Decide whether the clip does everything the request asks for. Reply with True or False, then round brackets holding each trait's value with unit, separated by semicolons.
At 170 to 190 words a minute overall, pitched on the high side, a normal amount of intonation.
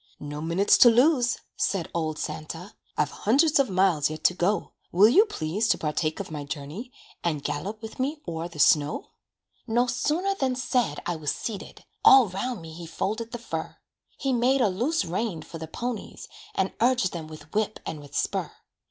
False (185 wpm; 195 Hz; 7.4 semitones)